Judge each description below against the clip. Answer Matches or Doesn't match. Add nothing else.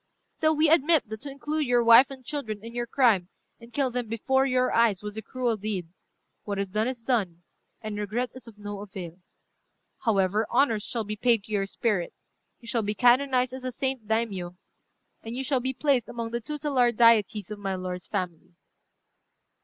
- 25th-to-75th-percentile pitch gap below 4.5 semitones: Matches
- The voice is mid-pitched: Doesn't match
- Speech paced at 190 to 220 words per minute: Matches